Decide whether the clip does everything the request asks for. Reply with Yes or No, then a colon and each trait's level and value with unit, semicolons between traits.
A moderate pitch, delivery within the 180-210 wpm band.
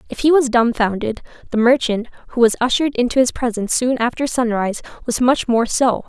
No: high, 240 Hz; average, 190 wpm